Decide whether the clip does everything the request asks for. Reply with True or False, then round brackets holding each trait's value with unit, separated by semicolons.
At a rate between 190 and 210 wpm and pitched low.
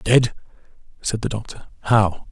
False (130 wpm; 110 Hz)